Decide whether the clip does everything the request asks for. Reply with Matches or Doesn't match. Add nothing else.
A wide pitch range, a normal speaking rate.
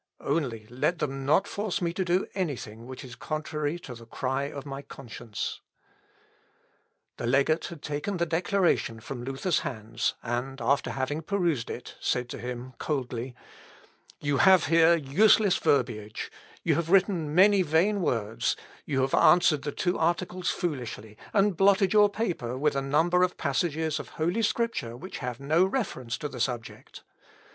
Matches